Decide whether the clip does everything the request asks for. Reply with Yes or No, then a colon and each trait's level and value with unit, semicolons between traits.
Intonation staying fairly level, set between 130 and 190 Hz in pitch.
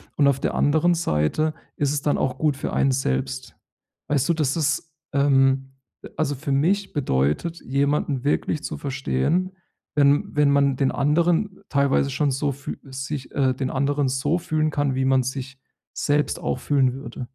Yes: narrow, 2.2 semitones; medium, 140 Hz